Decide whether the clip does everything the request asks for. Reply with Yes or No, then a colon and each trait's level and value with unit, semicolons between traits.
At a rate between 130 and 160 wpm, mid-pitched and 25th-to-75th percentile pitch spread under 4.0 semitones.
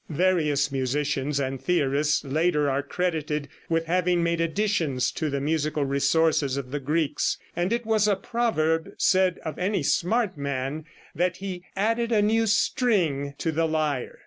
No: average, 155 wpm; medium, 160 Hz; average, 4.5 semitones